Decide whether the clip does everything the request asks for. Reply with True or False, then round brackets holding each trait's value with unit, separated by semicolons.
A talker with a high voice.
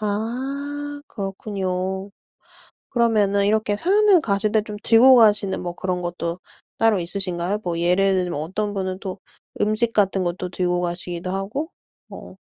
True (200 Hz)